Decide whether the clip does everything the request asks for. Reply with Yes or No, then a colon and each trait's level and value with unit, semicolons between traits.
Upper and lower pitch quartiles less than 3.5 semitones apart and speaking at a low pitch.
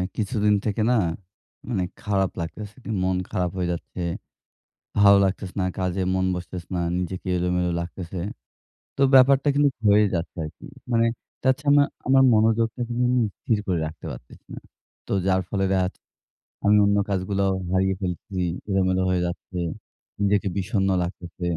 Yes: average, 2.9 semitones; very low, 95 Hz